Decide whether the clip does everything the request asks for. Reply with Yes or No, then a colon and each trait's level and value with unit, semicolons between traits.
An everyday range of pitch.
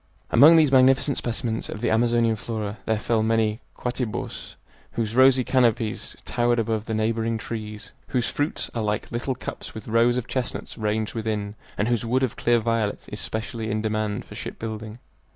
No: narrow, 1.8 semitones